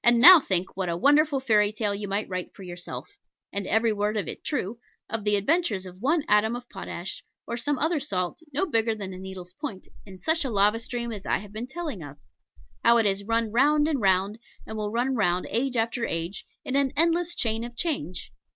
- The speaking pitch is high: Yes, high, 220 Hz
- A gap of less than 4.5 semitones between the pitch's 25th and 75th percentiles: No, wide, 5.4 semitones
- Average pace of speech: No, fast, 220 wpm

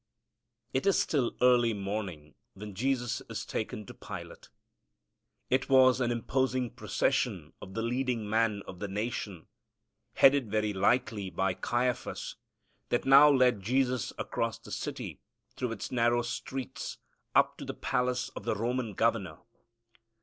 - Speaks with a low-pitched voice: Yes, low, 120 Hz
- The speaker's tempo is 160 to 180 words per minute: No, average, 140 wpm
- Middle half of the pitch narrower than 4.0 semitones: Yes, average, 3.5 semitones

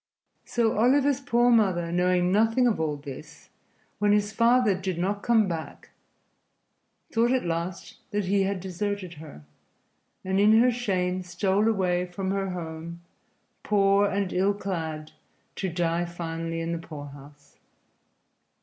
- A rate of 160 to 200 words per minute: No, average, 140 wpm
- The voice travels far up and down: No, average, 3.6 semitones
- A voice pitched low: No, high, 190 Hz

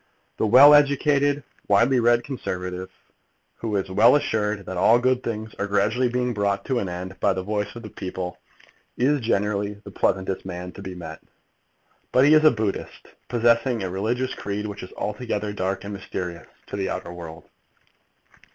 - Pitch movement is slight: No, average, 4.4 semitones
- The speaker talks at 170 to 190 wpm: Yes, average, 175 wpm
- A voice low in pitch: Yes, low, 105 Hz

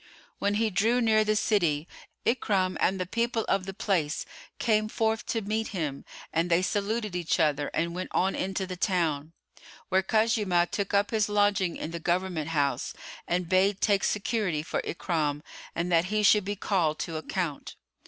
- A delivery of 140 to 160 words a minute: No, average, 175 wpm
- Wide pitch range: No, average, 3.8 semitones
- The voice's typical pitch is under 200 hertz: Yes, high, 190 Hz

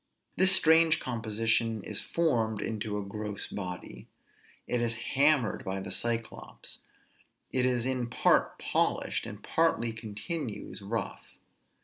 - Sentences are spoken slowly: Yes, slow, 125 wpm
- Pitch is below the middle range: Yes, low, 115 Hz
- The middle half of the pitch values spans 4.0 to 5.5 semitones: No, average, 3.4 semitones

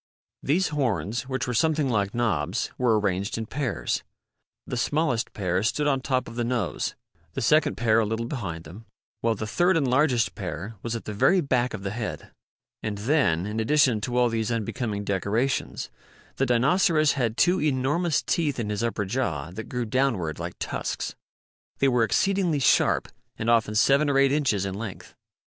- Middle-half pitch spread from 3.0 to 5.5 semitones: Yes, average, 4.5 semitones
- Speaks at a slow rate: No, average, 180 wpm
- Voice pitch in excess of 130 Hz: No, low, 120 Hz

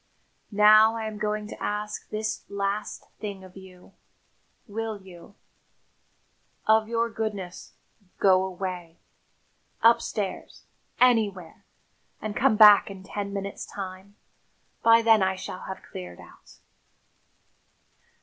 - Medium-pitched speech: No, high, 205 Hz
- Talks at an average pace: No, slow, 110 wpm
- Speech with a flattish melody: Yes, narrow, 2.3 semitones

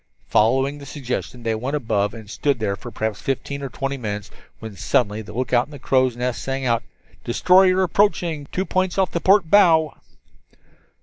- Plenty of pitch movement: Yes, wide, 5.7 semitones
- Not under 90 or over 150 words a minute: No, average, 185 wpm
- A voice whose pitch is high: No, low, 135 Hz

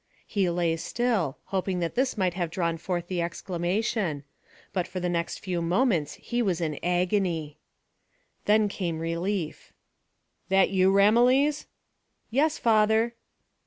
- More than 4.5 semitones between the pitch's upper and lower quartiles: No, average, 4.0 semitones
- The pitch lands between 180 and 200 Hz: Yes, medium, 185 Hz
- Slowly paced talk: Yes, slow, 130 wpm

